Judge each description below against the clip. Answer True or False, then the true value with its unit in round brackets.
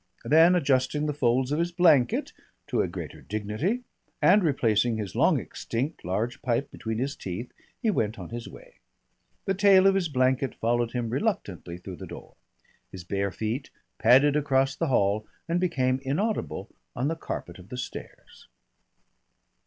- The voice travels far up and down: True (6.4 semitones)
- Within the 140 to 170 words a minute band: True (160 wpm)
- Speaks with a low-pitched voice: True (130 Hz)